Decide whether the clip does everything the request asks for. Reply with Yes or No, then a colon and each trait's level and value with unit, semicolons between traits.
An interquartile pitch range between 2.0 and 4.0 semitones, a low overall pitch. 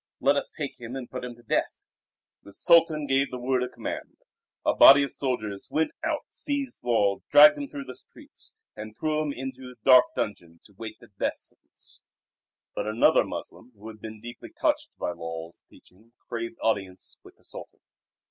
No: average, 4.6 semitones; low, 125 Hz